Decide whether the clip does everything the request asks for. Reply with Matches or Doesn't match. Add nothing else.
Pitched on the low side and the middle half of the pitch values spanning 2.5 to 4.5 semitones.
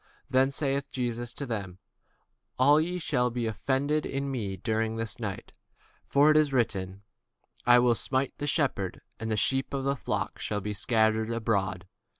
Matches